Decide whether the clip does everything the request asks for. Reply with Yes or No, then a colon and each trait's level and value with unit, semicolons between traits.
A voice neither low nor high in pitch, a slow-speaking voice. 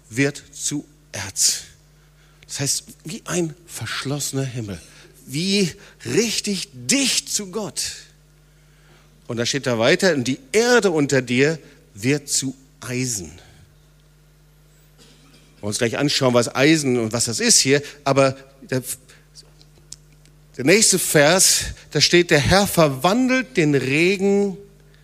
Yes: medium, 150 Hz; slow, 115 wpm